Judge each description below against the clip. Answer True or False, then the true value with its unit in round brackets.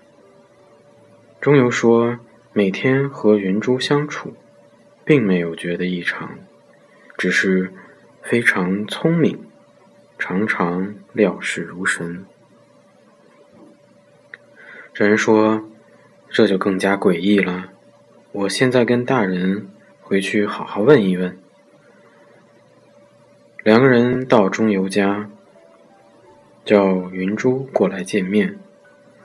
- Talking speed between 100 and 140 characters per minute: True (135 characters per minute)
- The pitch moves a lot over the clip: False (4.3 semitones)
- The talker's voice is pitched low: True (105 Hz)